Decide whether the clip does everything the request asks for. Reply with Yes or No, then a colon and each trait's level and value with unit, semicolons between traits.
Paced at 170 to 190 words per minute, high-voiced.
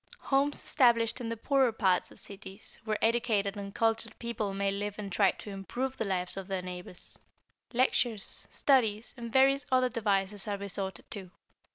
Yes: average, 175 wpm; high, 210 Hz